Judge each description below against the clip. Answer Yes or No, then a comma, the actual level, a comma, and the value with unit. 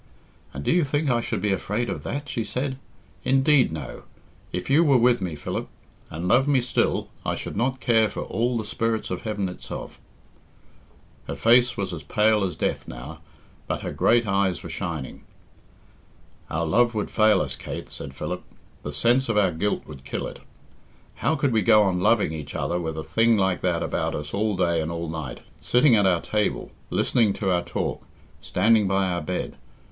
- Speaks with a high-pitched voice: No, low, 105 Hz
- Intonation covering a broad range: Yes, wide, 5.9 semitones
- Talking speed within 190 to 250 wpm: Yes, average, 195 wpm